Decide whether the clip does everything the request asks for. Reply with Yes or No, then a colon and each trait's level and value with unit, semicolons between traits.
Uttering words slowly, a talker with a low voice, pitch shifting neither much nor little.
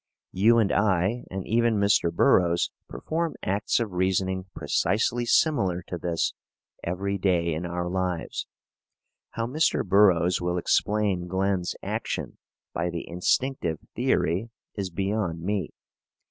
Yes: slow, 125 wpm; very low, 95 Hz; average, 3.1 semitones